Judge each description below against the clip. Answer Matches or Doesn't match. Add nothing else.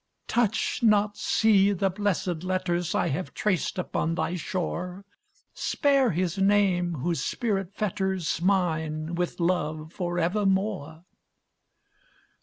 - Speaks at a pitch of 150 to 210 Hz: Matches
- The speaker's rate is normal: Doesn't match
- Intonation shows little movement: Doesn't match